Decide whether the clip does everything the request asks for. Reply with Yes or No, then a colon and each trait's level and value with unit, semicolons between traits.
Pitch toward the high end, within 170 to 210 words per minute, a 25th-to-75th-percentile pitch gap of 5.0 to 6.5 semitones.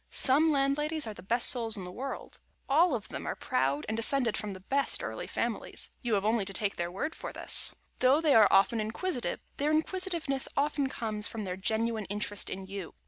Yes: high, 230 Hz; fast, 205 wpm; wide, 5.6 semitones